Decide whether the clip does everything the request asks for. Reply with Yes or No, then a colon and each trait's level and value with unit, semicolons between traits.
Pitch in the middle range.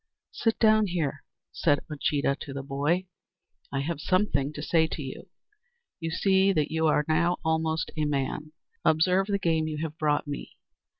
Yes: medium, 160 Hz